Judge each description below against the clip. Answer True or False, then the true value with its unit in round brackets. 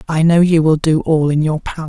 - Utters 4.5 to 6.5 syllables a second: True (5.7 syllables/s)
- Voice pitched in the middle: True (160 Hz)